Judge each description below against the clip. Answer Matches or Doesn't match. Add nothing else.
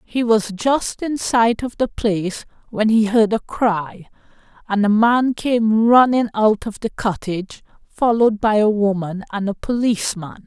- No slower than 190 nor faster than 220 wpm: Doesn't match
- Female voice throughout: Matches